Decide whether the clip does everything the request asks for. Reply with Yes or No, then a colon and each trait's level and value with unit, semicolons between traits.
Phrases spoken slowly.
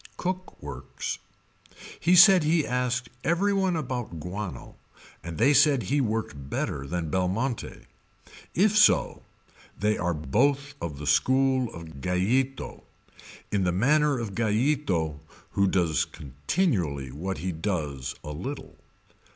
Yes: slow, 125 wpm